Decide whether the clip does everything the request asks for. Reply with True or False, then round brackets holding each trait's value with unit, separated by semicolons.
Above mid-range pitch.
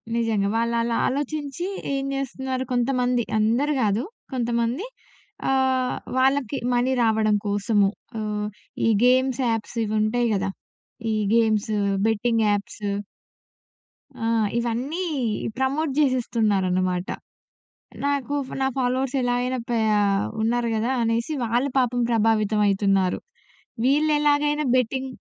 True (240 Hz)